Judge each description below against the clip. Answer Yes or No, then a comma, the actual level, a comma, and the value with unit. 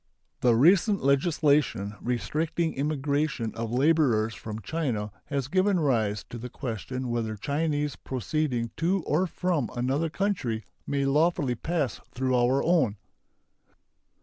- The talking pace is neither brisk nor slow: No, slow, 120 wpm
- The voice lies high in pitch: No, medium, 140 Hz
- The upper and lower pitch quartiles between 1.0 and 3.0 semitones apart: No, average, 5.1 semitones